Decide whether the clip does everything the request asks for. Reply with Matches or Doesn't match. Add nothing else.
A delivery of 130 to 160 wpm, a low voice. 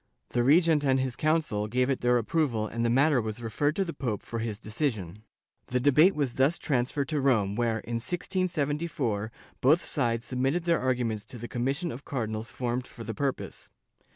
Doesn't match